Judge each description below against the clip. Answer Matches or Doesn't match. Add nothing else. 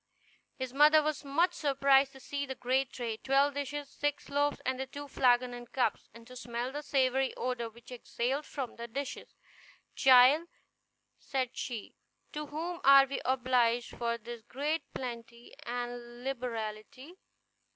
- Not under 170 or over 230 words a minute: Doesn't match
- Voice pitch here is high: Matches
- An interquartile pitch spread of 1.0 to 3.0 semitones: Matches